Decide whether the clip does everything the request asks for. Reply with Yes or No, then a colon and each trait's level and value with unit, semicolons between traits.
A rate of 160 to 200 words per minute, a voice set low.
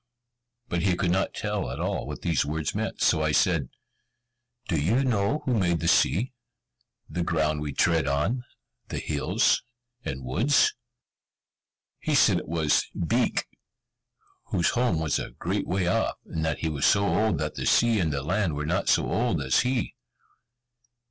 Yes: average, 170 wpm; very low, 85 Hz